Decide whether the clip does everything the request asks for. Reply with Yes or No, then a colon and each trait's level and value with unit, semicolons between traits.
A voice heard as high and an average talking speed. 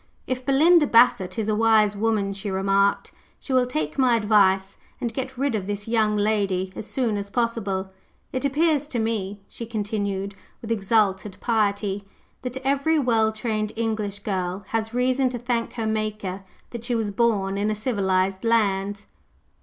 Yes: high, 215 Hz; average, 165 wpm